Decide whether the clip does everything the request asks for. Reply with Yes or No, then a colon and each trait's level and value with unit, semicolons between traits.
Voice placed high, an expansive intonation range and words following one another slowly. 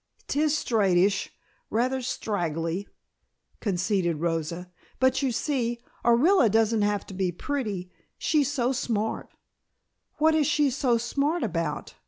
Yes: high, 225 Hz; wide, 6.4 semitones; slow, 120 wpm